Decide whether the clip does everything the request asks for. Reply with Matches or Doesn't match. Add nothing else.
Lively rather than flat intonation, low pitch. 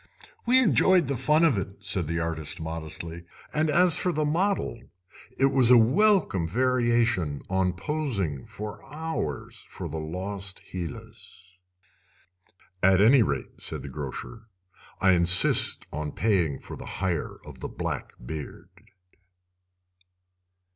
Matches